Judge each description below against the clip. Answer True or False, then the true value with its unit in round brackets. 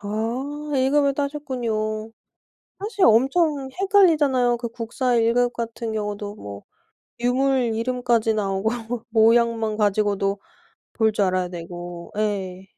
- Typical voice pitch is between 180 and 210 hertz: False (230 Hz)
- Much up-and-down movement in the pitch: False (3.7 semitones)